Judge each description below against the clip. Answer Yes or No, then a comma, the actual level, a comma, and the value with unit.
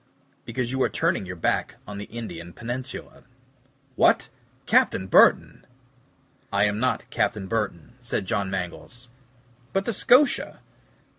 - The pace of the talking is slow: Yes, slow, 130 wpm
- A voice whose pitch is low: Yes, low, 105 Hz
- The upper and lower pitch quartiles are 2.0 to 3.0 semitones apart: No, average, 4.9 semitones